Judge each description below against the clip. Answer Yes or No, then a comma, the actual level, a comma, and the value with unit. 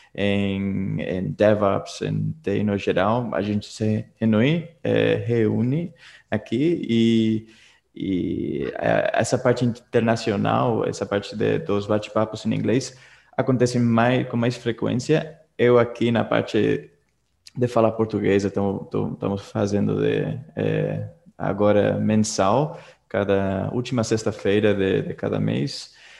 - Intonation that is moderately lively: Yes, average, 3.2 semitones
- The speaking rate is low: Yes, slow, 115 wpm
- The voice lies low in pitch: Yes, low, 110 Hz